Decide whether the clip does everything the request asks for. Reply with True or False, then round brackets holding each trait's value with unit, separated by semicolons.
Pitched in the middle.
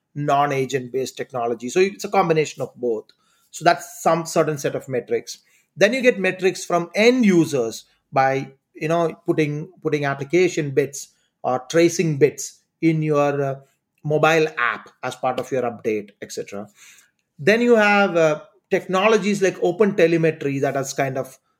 True (160 Hz)